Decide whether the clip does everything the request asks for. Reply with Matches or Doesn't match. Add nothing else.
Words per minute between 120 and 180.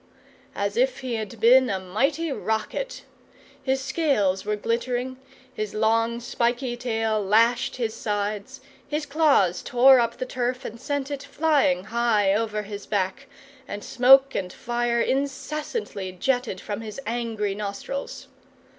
Matches